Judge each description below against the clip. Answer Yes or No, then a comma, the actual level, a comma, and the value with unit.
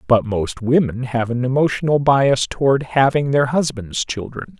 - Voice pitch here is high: No, low, 130 Hz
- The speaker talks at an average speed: Yes, average, 155 wpm